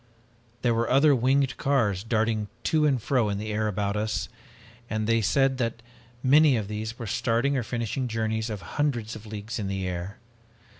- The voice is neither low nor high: No, low, 115 Hz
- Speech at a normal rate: Yes, average, 185 wpm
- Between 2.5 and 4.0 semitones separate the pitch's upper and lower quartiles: Yes, average, 3.3 semitones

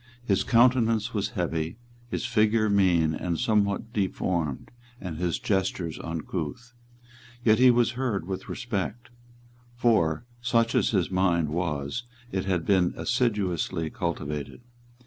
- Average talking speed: No, slow, 125 wpm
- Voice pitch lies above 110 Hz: No, very low, 95 Hz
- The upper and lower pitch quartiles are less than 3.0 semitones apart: No, average, 5.3 semitones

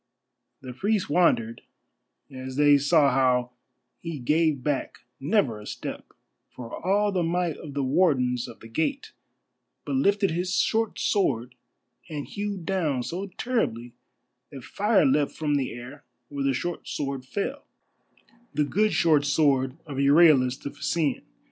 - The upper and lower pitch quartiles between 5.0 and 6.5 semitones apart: Yes, wide, 5.5 semitones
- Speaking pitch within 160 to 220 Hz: No, medium, 145 Hz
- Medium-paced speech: Yes, average, 145 wpm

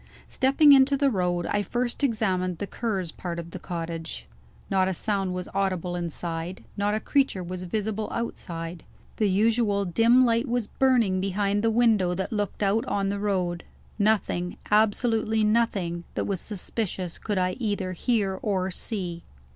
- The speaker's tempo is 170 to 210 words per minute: No, average, 160 wpm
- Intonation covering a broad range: No, average, 3.6 semitones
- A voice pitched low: No, high, 200 Hz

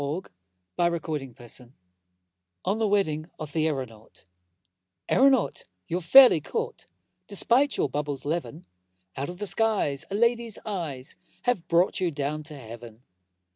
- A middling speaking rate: No, slow, 130 wpm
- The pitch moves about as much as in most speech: No, wide, 6.4 semitones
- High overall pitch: No, medium, 165 Hz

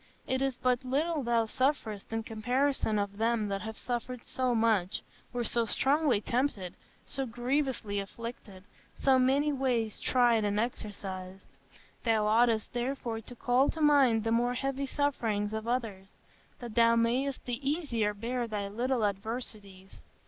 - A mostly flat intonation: No, average, 3.2 semitones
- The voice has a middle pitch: No, high, 235 Hz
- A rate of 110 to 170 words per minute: Yes, average, 150 wpm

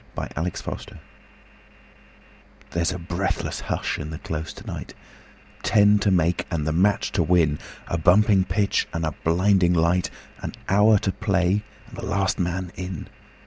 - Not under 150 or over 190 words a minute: Yes, average, 155 wpm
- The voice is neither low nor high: No, very low, 90 Hz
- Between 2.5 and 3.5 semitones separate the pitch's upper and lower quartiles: Yes, average, 2.8 semitones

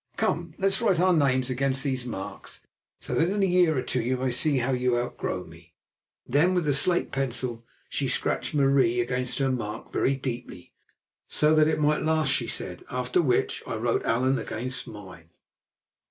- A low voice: Yes, low, 130 Hz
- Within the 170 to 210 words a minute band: Yes, average, 185 wpm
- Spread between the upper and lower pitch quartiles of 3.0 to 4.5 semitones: Yes, average, 4.0 semitones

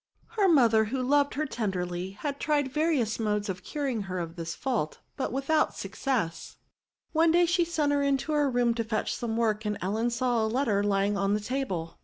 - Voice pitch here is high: Yes, high, 235 Hz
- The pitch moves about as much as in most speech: No, wide, 5.7 semitones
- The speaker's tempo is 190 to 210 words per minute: Yes, fast, 205 wpm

